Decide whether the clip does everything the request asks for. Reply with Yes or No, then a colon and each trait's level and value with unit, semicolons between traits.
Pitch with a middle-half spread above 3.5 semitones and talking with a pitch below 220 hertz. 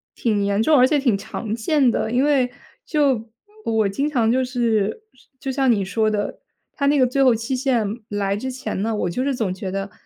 No: average, 4.1 semitones; high, 235 Hz